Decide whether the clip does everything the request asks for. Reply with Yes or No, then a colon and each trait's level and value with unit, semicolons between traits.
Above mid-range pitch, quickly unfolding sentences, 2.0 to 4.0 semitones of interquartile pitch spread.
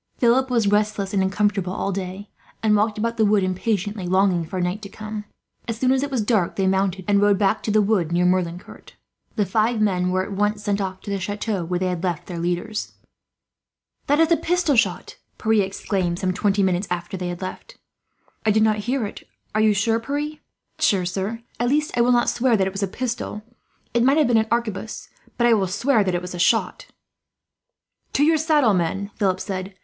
Yes: high, 205 Hz; fast, 215 wpm; average, 3.4 semitones